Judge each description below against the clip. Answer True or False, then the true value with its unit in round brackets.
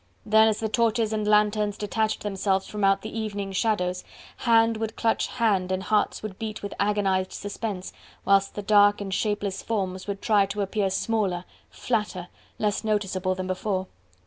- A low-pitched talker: False (205 Hz)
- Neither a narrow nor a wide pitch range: False (2.0 semitones)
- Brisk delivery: False (170 wpm)